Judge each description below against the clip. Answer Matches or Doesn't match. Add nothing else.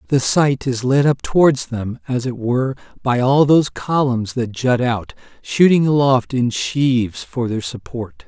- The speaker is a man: Matches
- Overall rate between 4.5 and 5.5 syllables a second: Doesn't match